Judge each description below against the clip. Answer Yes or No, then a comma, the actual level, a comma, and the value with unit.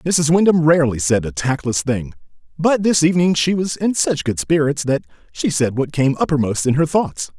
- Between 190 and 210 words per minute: Yes, fast, 205 wpm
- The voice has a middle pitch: Yes, medium, 150 Hz